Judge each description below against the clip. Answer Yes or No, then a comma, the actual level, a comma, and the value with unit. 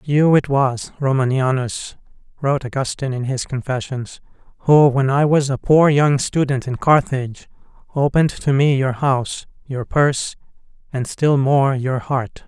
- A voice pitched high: No, low, 135 Hz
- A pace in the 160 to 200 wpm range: No, average, 150 wpm